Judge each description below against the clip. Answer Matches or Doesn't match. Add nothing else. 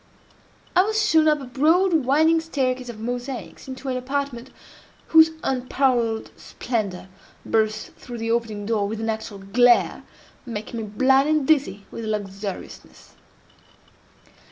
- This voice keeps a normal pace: Doesn't match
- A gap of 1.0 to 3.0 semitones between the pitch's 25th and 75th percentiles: Doesn't match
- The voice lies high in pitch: Matches